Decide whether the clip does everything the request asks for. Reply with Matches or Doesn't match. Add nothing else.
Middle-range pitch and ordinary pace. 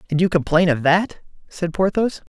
Matches